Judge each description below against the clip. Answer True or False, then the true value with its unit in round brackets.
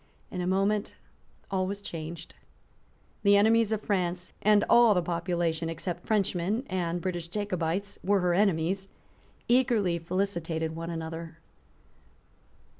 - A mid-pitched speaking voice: True (180 Hz)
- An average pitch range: True (3.2 semitones)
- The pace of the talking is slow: True (120 wpm)